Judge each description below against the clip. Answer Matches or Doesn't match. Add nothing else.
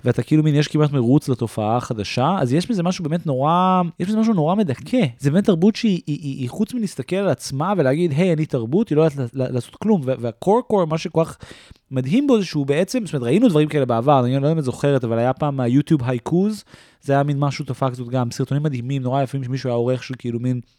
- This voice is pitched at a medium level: Matches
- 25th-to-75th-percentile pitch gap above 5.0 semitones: Matches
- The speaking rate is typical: Doesn't match